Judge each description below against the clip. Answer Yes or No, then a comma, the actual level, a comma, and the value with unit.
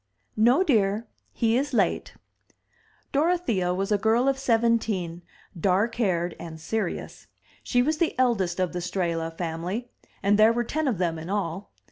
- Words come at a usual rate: Yes, average, 155 wpm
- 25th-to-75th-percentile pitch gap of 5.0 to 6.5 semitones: Yes, average, 5.3 semitones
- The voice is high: Yes, high, 205 Hz